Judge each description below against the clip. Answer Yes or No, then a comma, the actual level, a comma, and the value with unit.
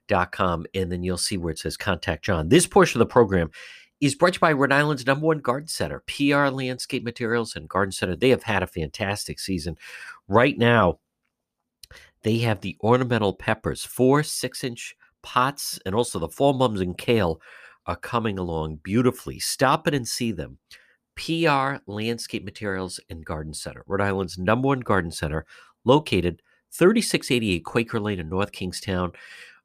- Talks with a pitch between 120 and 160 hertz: No, low, 110 Hz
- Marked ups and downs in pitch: Yes, wide, 5.7 semitones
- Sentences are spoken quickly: No, average, 170 wpm